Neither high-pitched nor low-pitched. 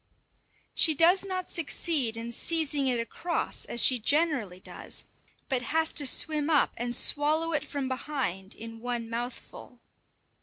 No: very high, 275 Hz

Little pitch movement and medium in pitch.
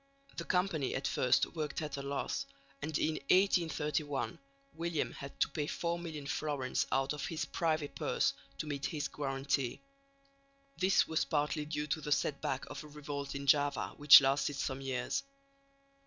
Yes: narrow, 2.1 semitones; medium, 145 Hz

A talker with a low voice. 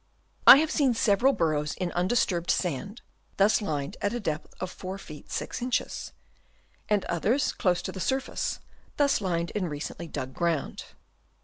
No: medium, 185 Hz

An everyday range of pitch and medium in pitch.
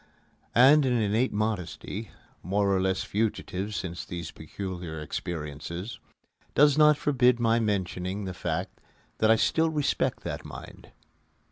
No: average, 4.8 semitones; low, 105 Hz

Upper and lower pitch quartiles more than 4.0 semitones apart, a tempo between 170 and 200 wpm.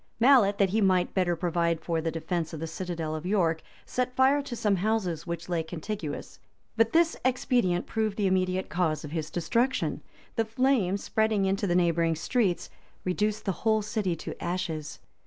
Yes: average, 4.5 semitones; average, 175 wpm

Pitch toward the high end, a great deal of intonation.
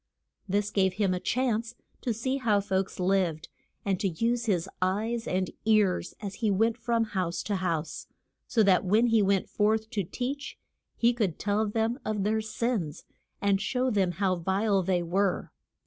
No: high, 205 Hz; average, 3.2 semitones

